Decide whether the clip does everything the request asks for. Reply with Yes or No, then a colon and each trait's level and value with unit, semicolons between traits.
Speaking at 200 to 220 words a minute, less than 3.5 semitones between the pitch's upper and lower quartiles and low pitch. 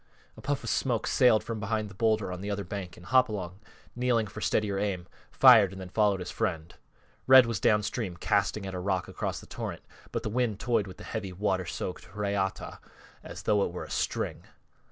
Yes: fast, 205 wpm; average, 3.1 semitones; low, 100 Hz